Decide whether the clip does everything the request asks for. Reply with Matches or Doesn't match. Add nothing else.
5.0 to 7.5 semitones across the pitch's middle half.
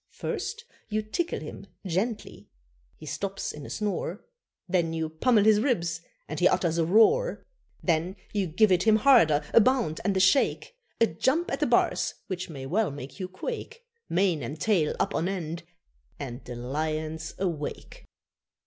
Matches